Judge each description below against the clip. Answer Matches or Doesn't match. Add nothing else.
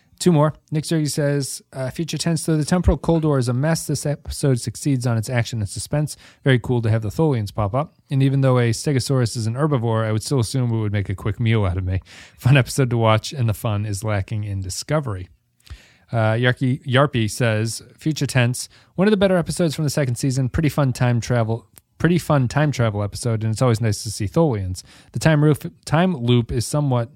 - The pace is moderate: Doesn't match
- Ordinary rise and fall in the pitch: Matches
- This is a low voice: Matches